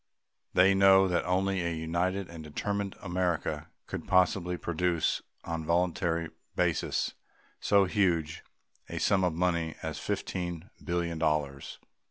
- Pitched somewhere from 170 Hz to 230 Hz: No, very low, 85 Hz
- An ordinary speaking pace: No, slow, 130 wpm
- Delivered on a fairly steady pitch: Yes, narrow, 2.2 semitones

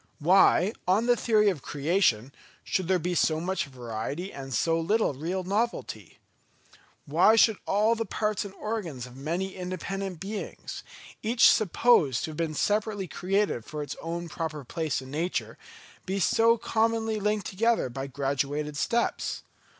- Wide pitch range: Yes, wide, 5.9 semitones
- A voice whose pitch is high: No, medium, 180 Hz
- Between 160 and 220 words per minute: No, average, 150 wpm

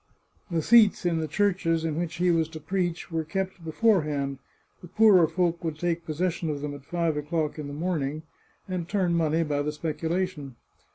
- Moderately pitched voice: Yes, medium, 165 Hz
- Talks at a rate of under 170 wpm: No, average, 185 wpm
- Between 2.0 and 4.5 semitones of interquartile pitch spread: Yes, average, 2.7 semitones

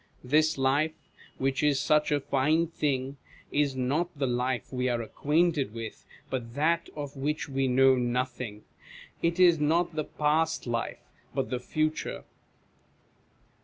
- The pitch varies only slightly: No, average, 3.3 semitones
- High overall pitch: No, medium, 140 Hz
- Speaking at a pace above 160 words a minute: No, average, 140 wpm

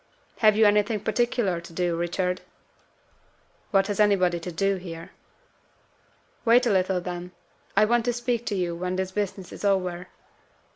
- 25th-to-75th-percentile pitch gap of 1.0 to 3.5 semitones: Yes, average, 3.0 semitones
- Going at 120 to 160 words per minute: Yes, average, 155 wpm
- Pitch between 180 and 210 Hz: Yes, high, 190 Hz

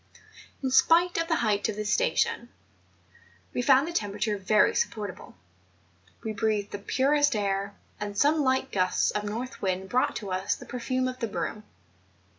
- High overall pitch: Yes, high, 215 Hz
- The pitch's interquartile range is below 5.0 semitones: Yes, average, 4.4 semitones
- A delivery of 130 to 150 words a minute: No, average, 165 wpm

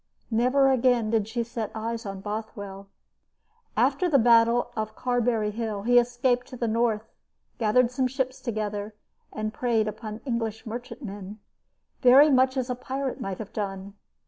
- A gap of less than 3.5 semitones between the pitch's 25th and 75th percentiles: Yes, average, 2.7 semitones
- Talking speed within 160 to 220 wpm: No, average, 150 wpm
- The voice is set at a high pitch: Yes, high, 230 Hz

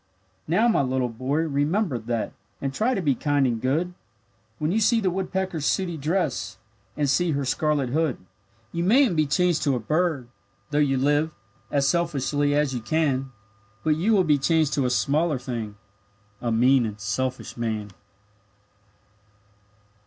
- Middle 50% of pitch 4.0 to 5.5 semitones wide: Yes, average, 4.7 semitones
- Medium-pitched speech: Yes, medium, 145 Hz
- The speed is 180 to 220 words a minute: No, average, 165 wpm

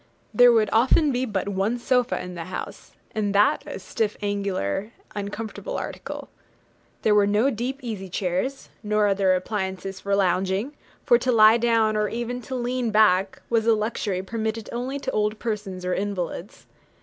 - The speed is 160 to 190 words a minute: Yes, average, 165 wpm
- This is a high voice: Yes, high, 210 Hz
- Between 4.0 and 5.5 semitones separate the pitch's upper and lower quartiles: No, average, 3.4 semitones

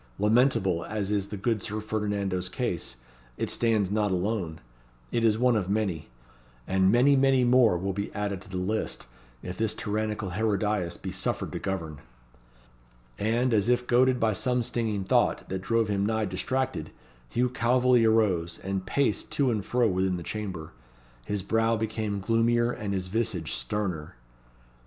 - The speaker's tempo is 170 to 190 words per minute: No, average, 160 wpm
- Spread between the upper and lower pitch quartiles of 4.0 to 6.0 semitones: No, average, 3.4 semitones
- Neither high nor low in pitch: No, low, 105 Hz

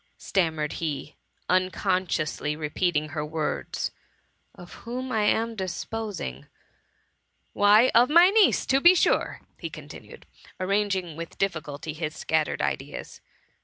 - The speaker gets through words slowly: Yes, slow, 125 wpm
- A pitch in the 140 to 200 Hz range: Yes, medium, 185 Hz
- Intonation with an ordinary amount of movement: No, wide, 6.1 semitones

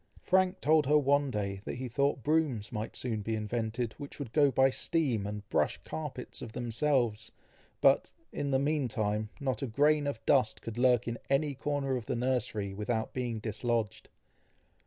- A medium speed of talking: Yes, average, 175 wpm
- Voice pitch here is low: Yes, low, 125 Hz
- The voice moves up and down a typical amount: Yes, average, 4.4 semitones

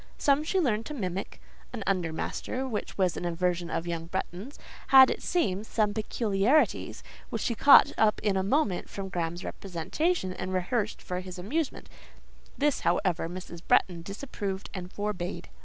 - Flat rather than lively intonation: No, average, 4.8 semitones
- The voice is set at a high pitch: Yes, high, 195 Hz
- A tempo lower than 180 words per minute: Yes, average, 160 wpm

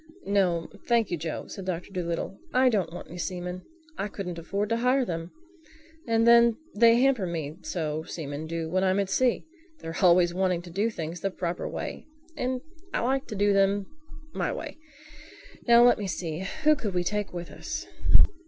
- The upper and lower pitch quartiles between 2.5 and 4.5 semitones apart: No, average, 5.1 semitones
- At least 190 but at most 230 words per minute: No, average, 180 wpm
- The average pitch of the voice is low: No, high, 195 Hz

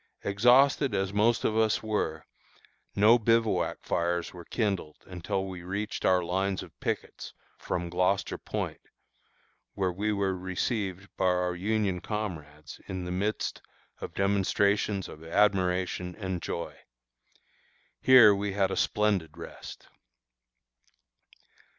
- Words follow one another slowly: Yes, slow, 120 wpm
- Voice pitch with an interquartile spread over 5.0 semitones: No, average, 2.7 semitones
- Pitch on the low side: Yes, very low, 95 Hz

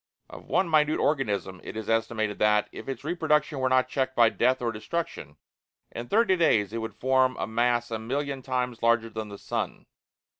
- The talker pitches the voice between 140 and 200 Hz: No, low, 120 Hz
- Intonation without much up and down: No, average, 3.6 semitones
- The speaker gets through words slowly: No, average, 190 wpm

